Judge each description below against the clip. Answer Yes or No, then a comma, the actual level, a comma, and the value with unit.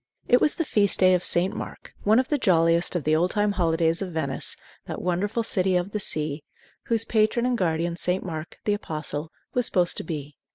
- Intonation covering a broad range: No, average, 4.2 semitones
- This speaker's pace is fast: Yes, fast, 210 wpm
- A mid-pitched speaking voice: Yes, medium, 180 Hz